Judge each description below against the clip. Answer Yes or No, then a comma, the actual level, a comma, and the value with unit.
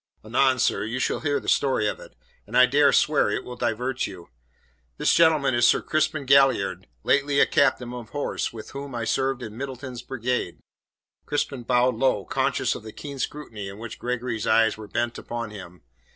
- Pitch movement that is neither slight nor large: Yes, average, 3.5 semitones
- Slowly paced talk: No, average, 190 wpm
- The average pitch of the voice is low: Yes, low, 125 Hz